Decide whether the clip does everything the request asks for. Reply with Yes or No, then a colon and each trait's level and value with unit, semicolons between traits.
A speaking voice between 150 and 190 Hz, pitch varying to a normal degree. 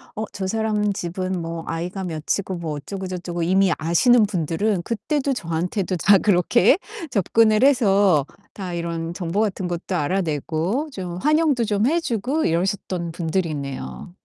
Yes: medium, 185 Hz; average, 4.1 semitones